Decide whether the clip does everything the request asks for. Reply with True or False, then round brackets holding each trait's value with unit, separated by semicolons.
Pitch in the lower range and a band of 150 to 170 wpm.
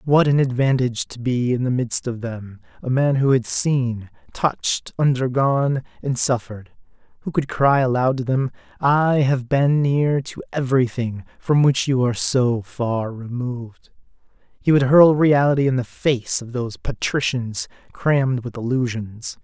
True (130 Hz; 155 wpm)